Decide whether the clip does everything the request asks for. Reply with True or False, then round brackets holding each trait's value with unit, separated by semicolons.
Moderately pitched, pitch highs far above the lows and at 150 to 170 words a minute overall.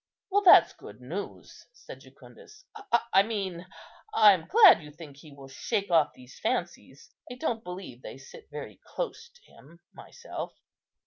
True (180 Hz; 8.6 semitones; 155 wpm)